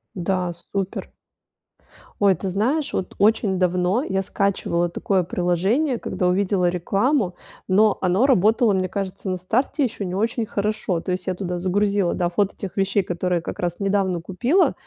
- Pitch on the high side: Yes, high, 195 Hz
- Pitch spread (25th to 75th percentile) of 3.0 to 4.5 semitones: No, narrow, 2.5 semitones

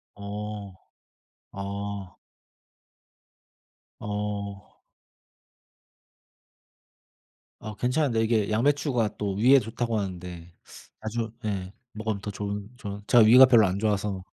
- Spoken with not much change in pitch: Yes, narrow, 2.1 semitones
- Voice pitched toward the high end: No, low, 105 Hz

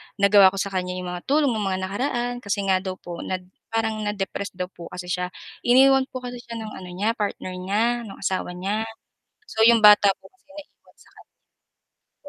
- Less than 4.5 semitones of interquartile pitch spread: Yes, average, 3.6 semitones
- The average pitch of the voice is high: Yes, high, 200 Hz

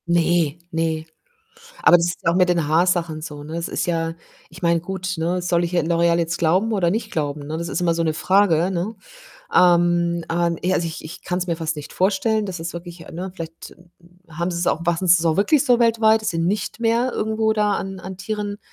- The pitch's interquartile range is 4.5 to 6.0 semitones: No, narrow, 2.4 semitones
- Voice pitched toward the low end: No, medium, 175 Hz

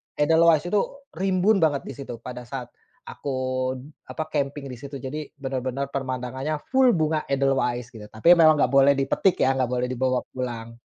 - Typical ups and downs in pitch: Yes, average, 3.4 semitones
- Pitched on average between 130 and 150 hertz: Yes, low, 135 Hz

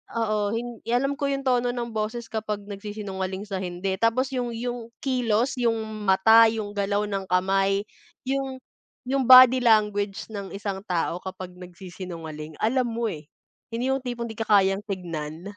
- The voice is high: Yes, high, 215 Hz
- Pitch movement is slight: No, average, 3.9 semitones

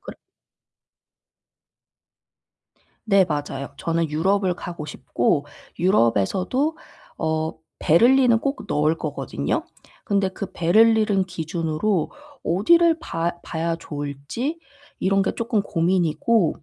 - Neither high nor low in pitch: Yes, medium, 175 Hz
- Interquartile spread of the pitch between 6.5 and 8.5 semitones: No, average, 5.3 semitones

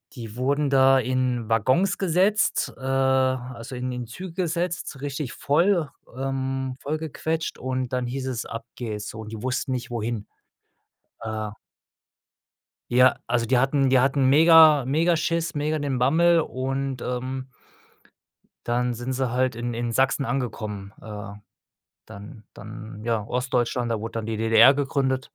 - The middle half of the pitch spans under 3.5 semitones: Yes, average, 2.9 semitones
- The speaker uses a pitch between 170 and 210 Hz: No, low, 130 Hz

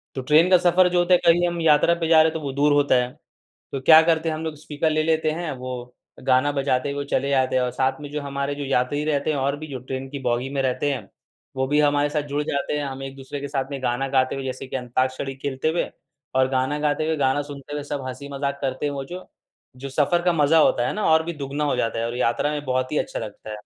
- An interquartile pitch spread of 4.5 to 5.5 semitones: No, narrow, 2.6 semitones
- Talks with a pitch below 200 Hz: Yes, medium, 140 Hz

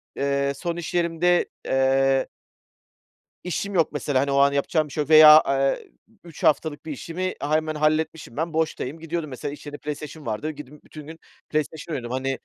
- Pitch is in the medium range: Yes, medium, 150 Hz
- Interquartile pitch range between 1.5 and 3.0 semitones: Yes, narrow, 2.5 semitones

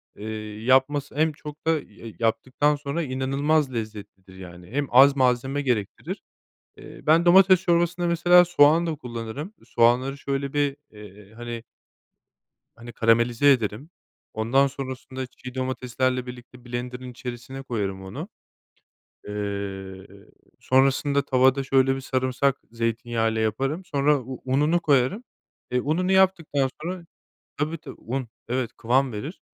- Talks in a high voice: No, low, 130 Hz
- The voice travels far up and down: No, average, 3.7 semitones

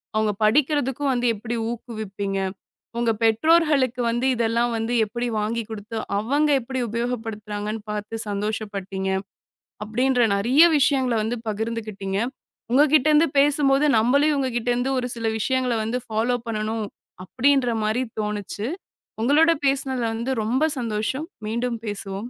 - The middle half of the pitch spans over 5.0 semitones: No, average, 3.4 semitones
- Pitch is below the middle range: No, high, 235 Hz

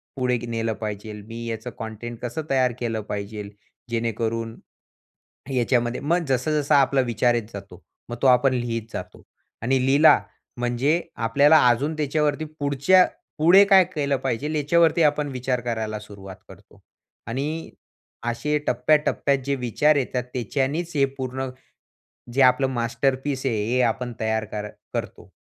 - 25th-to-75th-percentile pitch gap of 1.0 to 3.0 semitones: No, average, 3.7 semitones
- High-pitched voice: No, low, 125 Hz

